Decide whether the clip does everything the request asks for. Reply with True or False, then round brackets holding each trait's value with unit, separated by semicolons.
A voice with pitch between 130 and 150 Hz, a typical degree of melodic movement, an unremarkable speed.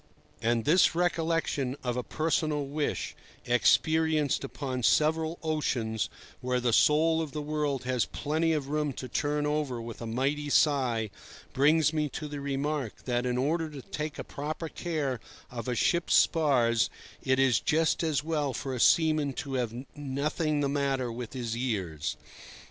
True (140 Hz; 3.5 semitones; 160 wpm)